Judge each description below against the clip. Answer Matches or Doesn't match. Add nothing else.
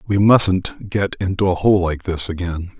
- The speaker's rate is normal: Matches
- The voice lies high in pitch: Doesn't match